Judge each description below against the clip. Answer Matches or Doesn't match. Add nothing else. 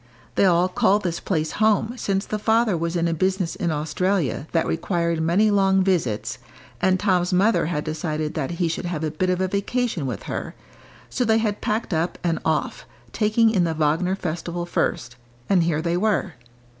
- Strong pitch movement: Doesn't match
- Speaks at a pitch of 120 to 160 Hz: Doesn't match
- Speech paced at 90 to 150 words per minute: Doesn't match